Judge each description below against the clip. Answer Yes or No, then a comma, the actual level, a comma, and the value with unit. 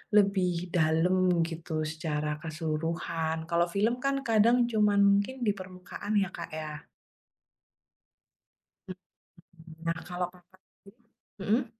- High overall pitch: No, medium, 180 Hz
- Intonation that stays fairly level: No, average, 3.9 semitones